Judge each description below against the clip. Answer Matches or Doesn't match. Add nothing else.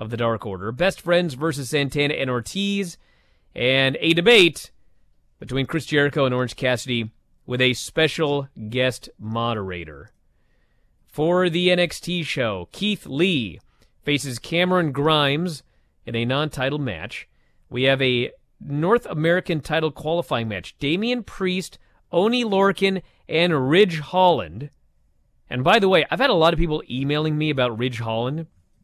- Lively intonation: Matches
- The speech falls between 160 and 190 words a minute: Doesn't match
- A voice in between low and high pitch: Matches